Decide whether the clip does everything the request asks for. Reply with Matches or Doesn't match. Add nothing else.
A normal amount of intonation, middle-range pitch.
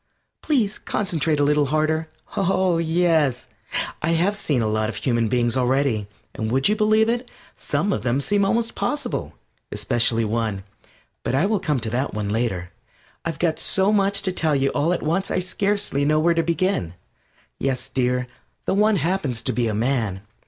Doesn't match